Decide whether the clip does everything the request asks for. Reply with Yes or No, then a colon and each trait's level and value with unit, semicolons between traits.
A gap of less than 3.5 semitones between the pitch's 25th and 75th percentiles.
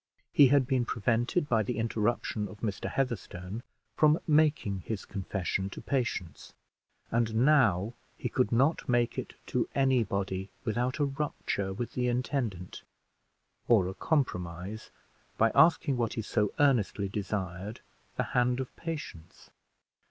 No: average, 4.9 semitones